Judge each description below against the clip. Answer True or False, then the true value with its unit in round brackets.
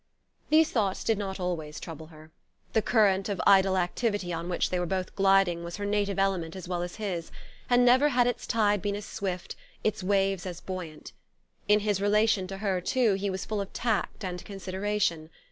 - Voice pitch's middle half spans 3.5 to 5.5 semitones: False (2.6 semitones)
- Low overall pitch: False (195 Hz)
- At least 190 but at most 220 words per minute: True (195 wpm)